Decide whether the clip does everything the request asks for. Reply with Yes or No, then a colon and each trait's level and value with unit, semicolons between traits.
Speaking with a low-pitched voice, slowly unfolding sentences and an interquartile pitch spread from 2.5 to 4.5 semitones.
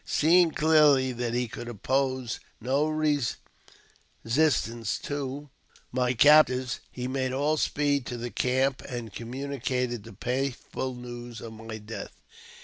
Yes: low, 130 Hz; slow, 130 wpm; average, 2.9 semitones